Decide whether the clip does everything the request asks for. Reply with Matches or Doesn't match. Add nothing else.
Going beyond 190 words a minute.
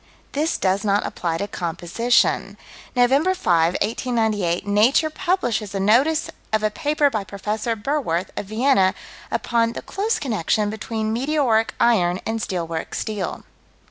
Doesn't match